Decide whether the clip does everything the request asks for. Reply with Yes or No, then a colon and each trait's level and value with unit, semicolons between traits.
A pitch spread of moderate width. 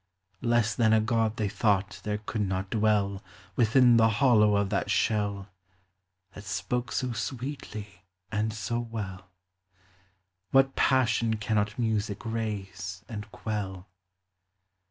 No: narrow, 2.2 semitones